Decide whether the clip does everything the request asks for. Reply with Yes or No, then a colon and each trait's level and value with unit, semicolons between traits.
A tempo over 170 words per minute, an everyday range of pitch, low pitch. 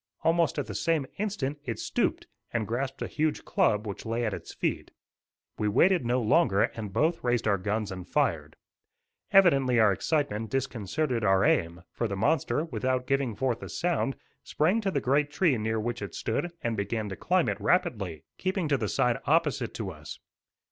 No: average, 185 wpm; wide, 6.2 semitones; low, 125 Hz